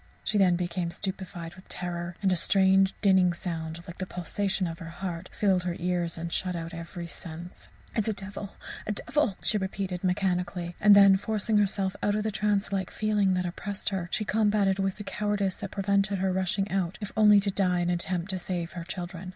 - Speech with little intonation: Yes, narrow, 2.3 semitones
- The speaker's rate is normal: No, fast, 210 wpm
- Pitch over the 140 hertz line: Yes, high, 190 Hz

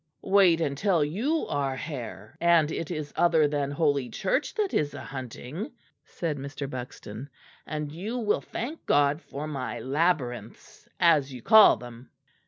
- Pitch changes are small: No, average, 4.2 semitones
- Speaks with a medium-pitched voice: Yes, medium, 150 Hz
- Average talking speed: Yes, average, 150 wpm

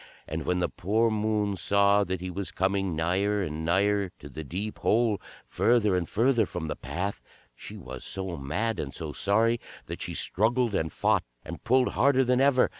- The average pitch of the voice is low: Yes, low, 100 Hz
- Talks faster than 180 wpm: Yes, average, 190 wpm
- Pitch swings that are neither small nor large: Yes, average, 4.2 semitones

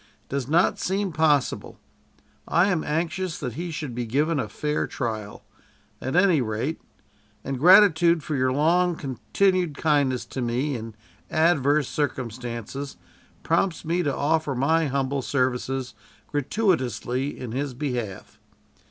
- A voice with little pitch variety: No, average, 4.4 semitones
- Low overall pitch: No, medium, 145 Hz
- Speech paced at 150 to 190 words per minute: No, slow, 135 wpm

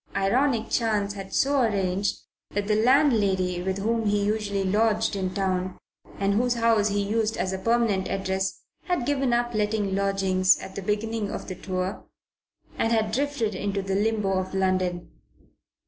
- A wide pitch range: No, average, 2.8 semitones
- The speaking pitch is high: Yes, high, 205 Hz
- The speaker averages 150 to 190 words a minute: Yes, average, 165 wpm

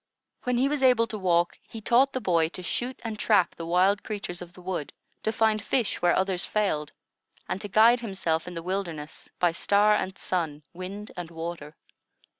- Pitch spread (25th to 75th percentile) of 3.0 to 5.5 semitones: Yes, average, 4.0 semitones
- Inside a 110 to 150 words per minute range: No, average, 195 wpm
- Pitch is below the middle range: No, high, 190 Hz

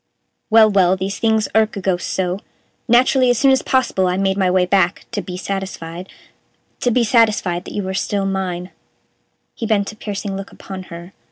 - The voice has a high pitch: Yes, high, 195 Hz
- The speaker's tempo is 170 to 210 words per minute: Yes, average, 190 wpm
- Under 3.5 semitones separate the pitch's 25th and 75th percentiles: Yes, average, 2.9 semitones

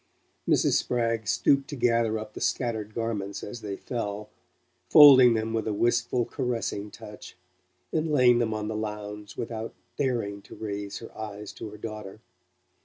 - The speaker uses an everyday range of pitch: No, narrow, 2.2 semitones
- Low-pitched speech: Yes, low, 110 Hz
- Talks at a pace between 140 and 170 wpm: Yes, average, 160 wpm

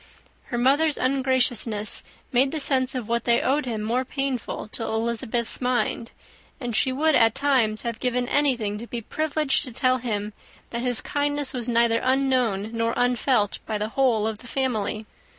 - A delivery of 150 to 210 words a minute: Yes, average, 170 wpm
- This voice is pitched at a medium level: No, high, 245 Hz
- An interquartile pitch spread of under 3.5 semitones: Yes, average, 2.8 semitones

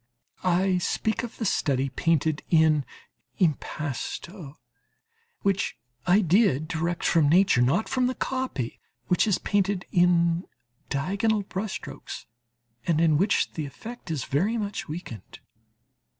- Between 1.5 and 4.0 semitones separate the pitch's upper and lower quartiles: No, average, 4.8 semitones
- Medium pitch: Yes, medium, 175 Hz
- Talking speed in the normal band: No, slow, 125 wpm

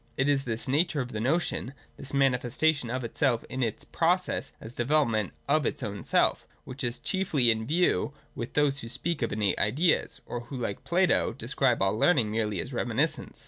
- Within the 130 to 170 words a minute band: No, average, 180 wpm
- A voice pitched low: Yes, low, 130 Hz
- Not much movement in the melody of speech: No, average, 4.4 semitones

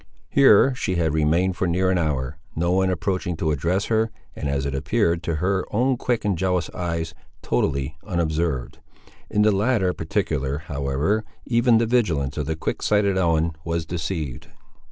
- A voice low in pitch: Yes, very low, 85 Hz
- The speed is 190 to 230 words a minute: No, average, 170 wpm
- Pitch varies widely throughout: No, average, 4.1 semitones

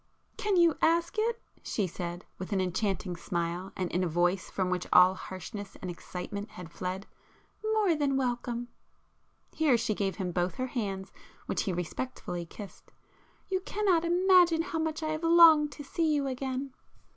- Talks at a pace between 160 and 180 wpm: Yes, average, 170 wpm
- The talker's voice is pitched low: No, high, 235 Hz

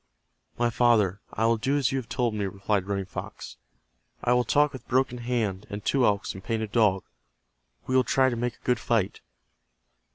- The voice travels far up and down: No, average, 3.4 semitones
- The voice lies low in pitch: Yes, low, 115 Hz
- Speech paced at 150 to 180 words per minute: No, average, 195 wpm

